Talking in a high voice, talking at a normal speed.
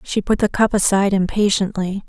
Yes: high, 200 Hz; average, 175 wpm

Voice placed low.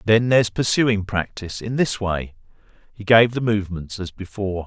Yes: low, 105 Hz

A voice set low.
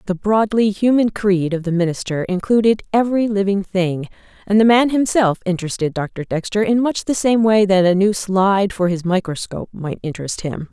No: high, 195 Hz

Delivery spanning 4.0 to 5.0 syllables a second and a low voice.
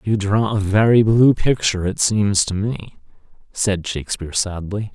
Yes: 4.6 syllables/s; low, 100 Hz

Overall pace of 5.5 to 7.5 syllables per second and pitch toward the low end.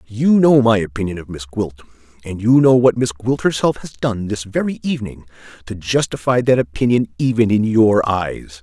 No: 5.0 syllables/s; low, 110 Hz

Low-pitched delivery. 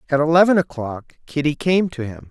No: medium, 150 Hz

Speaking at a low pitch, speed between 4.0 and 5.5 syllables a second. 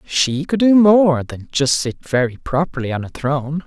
No: medium, 150 Hz; 4.6 syllables/s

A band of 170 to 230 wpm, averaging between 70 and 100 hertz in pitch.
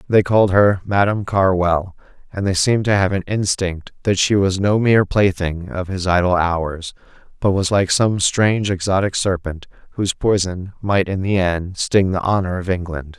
Yes: average, 180 wpm; very low, 95 Hz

